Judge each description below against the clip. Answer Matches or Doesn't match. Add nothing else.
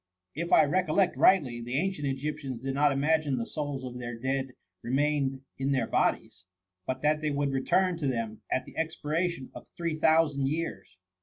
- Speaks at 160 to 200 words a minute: Matches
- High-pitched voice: Doesn't match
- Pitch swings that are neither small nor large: Matches